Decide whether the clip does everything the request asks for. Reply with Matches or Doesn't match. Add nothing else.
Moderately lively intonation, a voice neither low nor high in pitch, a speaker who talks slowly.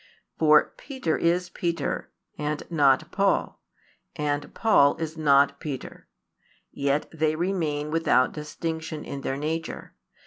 Doesn't match